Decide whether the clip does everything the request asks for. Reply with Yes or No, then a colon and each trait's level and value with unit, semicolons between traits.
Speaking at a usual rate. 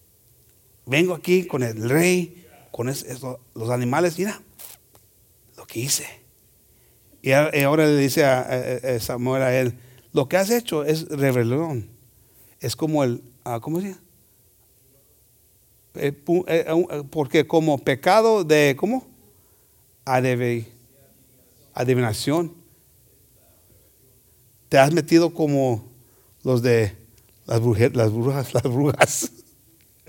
No: slow, 100 wpm